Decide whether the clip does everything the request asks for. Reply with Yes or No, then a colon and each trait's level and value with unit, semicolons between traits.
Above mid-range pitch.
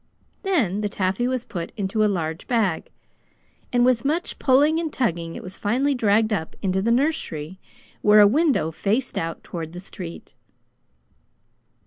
Yes: high, 210 Hz